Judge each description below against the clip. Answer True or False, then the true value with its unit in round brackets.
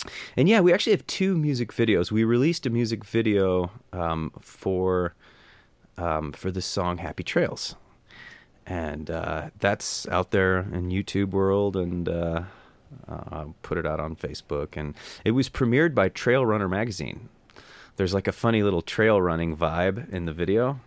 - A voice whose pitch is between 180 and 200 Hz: False (95 Hz)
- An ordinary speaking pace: True (165 wpm)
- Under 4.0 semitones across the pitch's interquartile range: False (4.9 semitones)